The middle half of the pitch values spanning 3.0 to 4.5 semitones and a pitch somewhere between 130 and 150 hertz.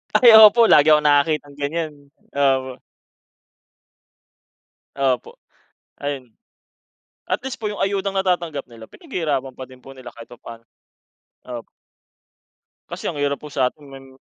Yes: average, 4.1 semitones; medium, 140 Hz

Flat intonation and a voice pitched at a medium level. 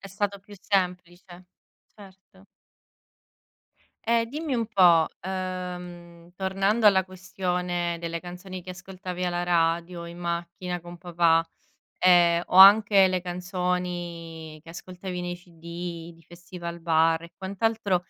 Yes: narrow, 1.7 semitones; medium, 180 Hz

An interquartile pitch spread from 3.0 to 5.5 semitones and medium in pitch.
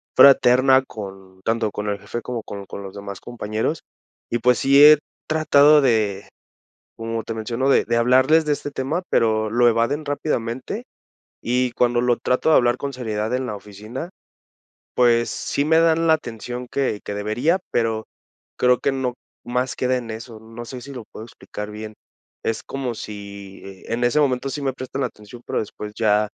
No: average, 3.5 semitones; low, 120 Hz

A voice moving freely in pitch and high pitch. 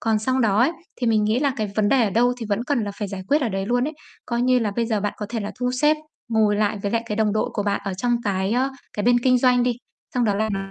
No: average, 3.1 semitones; high, 225 Hz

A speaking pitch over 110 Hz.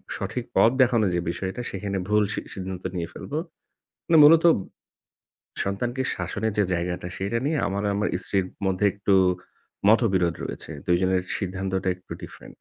No: low, 100 Hz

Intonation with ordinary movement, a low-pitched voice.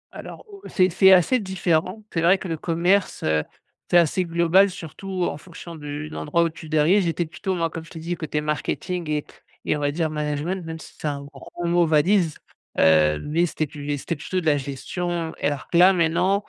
No: average, 3.1 semitones; medium, 165 Hz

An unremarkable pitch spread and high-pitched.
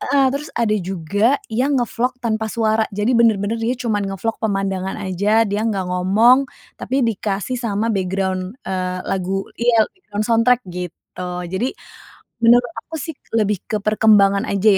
Yes: average, 3.3 semitones; high, 215 Hz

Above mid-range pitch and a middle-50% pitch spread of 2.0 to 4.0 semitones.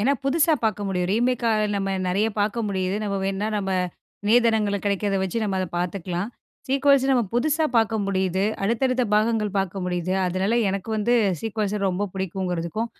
Yes: high, 205 Hz; average, 3.2 semitones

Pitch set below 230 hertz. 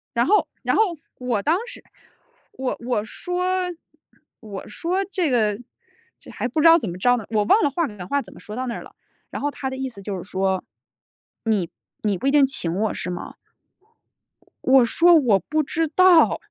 No: very high, 255 Hz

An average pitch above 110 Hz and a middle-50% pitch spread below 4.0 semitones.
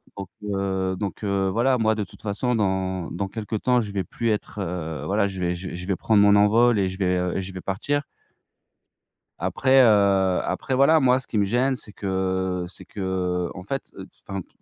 No: low, 100 Hz; average, 2.9 semitones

